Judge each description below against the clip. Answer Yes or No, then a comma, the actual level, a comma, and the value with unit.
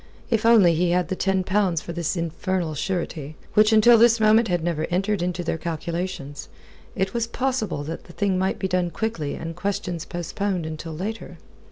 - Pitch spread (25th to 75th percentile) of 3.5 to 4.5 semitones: Yes, average, 3.8 semitones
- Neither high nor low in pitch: Yes, medium, 180 Hz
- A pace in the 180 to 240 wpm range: Yes, average, 185 wpm